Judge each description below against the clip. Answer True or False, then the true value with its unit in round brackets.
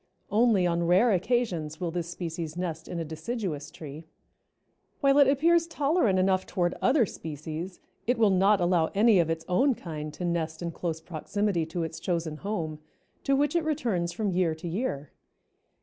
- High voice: False (180 Hz)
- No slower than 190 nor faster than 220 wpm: False (175 wpm)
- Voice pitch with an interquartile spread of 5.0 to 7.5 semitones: True (5.3 semitones)